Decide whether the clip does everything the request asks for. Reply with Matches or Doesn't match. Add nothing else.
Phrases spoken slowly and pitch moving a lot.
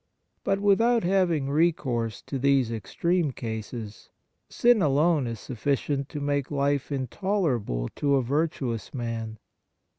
Matches